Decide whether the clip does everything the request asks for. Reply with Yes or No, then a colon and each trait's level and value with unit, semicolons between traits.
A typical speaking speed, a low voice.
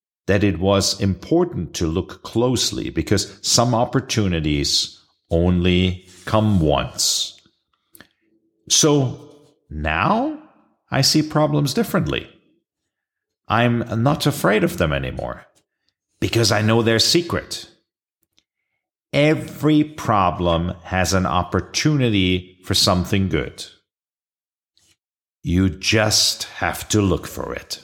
No: slow, 95 wpm; low, 105 Hz